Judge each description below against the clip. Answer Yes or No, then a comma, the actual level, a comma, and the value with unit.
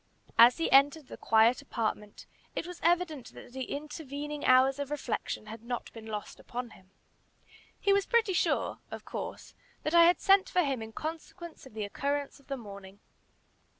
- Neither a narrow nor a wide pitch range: No, wide, 5.9 semitones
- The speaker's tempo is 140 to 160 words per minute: No, average, 180 wpm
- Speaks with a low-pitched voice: No, very high, 275 Hz